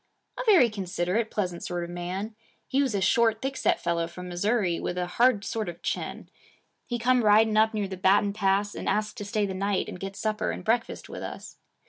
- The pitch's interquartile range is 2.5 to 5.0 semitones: Yes, average, 3.4 semitones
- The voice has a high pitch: Yes, high, 205 Hz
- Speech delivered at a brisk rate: Yes, fast, 215 wpm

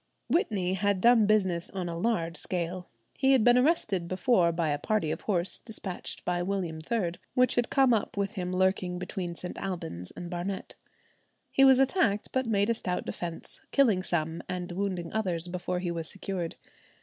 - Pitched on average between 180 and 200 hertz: Yes, medium, 185 Hz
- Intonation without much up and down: No, average, 3.7 semitones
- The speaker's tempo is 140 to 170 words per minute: No, average, 180 wpm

